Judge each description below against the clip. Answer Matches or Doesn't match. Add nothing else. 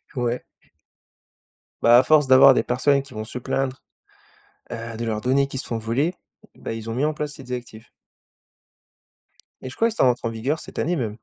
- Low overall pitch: Matches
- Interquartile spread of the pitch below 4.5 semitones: Matches